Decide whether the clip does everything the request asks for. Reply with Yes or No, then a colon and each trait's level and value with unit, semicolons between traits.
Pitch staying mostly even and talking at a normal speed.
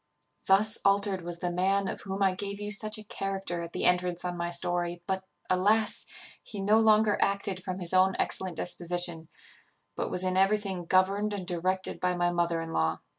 Yes: narrow, 2.2 semitones; average, 190 wpm